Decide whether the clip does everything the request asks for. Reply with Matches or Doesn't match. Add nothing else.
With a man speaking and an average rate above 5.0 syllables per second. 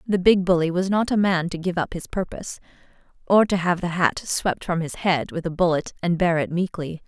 Doesn't match